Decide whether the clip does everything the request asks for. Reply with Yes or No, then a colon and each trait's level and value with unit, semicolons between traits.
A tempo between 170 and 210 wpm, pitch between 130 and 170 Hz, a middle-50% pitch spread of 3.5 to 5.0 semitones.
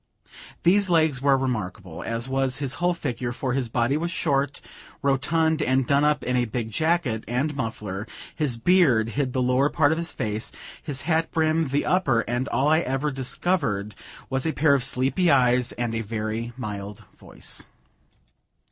Yes: average, 175 wpm; low, 135 Hz; average, 4.5 semitones